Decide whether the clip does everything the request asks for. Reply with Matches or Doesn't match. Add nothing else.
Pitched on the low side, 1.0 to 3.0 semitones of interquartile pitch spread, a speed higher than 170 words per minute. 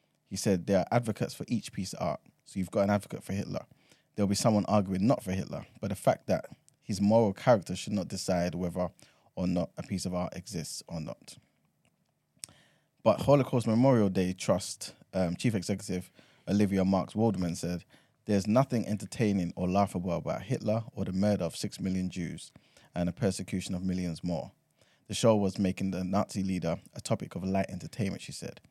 Matches